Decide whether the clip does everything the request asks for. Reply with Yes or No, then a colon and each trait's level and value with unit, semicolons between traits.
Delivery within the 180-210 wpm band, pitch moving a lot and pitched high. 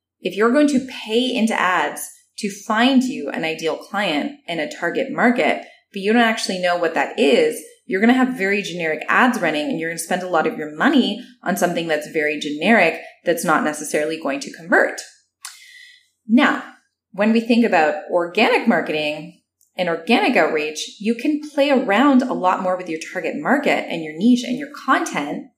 Yes: average, 190 wpm; wide, 7.5 semitones; high, 215 Hz